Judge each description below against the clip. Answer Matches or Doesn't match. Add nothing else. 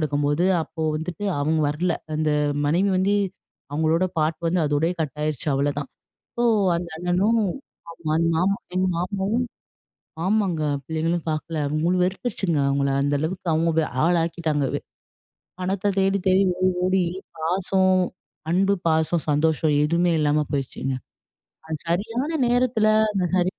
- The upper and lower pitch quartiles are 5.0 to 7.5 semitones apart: Doesn't match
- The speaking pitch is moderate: Matches